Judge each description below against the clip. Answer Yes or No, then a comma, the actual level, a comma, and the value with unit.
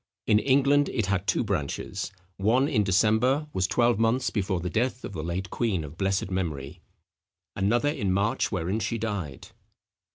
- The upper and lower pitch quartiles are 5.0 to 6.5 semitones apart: No, average, 4.2 semitones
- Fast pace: No, average, 165 wpm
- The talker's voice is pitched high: No, low, 105 Hz